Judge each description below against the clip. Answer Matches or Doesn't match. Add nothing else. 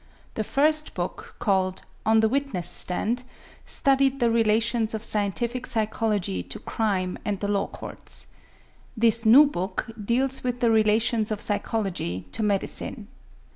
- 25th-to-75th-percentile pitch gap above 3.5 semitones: Doesn't match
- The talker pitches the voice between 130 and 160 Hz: Doesn't match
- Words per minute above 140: Doesn't match